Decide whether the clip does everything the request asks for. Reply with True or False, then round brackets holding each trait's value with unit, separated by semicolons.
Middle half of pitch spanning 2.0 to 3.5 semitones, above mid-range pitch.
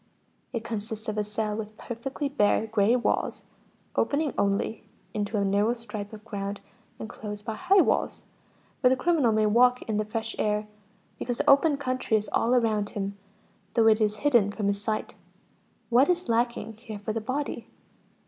True (2.8 semitones; 220 Hz)